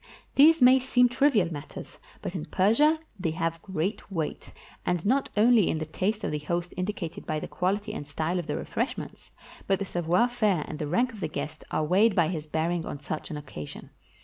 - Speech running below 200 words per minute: No, fast, 205 wpm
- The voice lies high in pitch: No, medium, 180 Hz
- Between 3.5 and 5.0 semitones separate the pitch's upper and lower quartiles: No, wide, 5.5 semitones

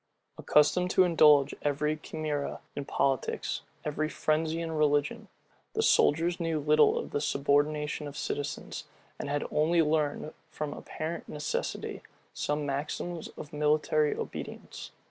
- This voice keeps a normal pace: No, slow, 125 wpm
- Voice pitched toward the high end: No, medium, 150 Hz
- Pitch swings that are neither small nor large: No, narrow, 1.2 semitones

